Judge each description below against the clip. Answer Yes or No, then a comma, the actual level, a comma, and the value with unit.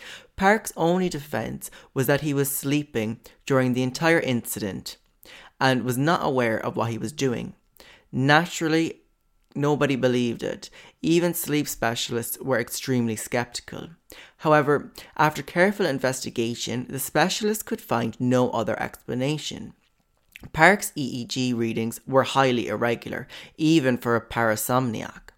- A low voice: Yes, low, 130 Hz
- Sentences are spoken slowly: Yes, slow, 125 wpm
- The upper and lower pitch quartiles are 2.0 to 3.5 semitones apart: No, average, 4.4 semitones